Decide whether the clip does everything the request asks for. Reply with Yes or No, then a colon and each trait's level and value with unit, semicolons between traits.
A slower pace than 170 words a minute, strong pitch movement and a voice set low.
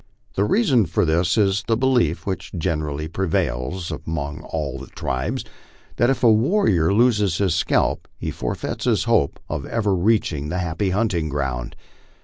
Yes: average, 155 wpm; wide, 5.7 semitones; very low, 90 Hz